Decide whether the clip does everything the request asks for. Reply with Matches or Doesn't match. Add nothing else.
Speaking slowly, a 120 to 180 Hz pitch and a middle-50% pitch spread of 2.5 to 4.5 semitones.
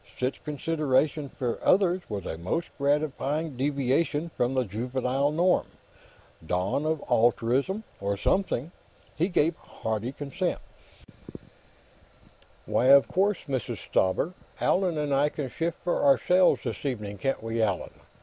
Doesn't match